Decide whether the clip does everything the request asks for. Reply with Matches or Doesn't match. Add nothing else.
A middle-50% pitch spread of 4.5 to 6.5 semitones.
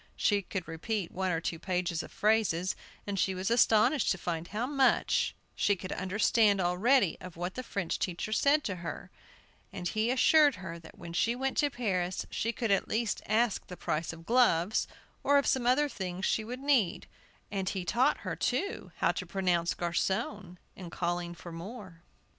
Matches